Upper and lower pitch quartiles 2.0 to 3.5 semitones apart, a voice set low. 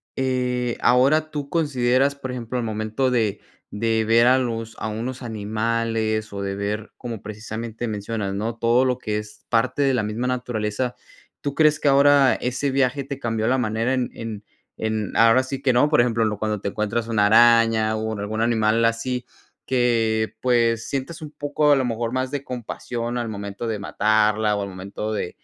Yes: average, 2.8 semitones; low, 115 Hz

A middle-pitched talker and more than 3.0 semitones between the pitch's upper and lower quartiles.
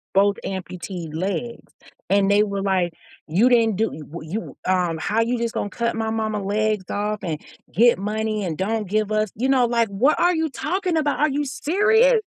No: high, 215 Hz; average, 3.7 semitones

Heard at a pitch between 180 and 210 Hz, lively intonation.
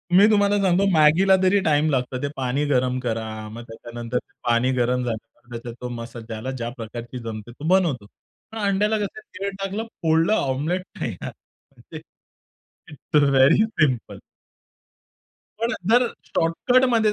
No: medium, 140 Hz; wide, 8.4 semitones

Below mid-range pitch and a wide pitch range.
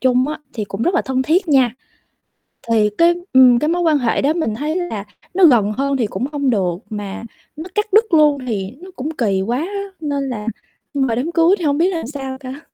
No: very high, 270 Hz; wide, 5.8 semitones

